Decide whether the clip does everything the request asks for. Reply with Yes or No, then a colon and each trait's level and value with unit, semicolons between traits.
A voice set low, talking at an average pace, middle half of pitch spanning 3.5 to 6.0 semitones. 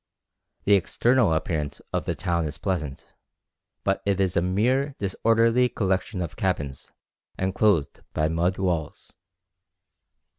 No: very low, 95 Hz; slow, 120 wpm; average, 4.2 semitones